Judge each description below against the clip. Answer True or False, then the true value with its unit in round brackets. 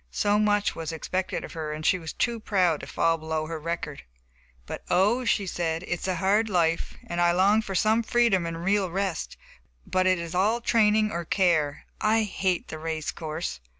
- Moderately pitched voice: True (180 Hz)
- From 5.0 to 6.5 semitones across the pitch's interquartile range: False (4.0 semitones)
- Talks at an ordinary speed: True (195 wpm)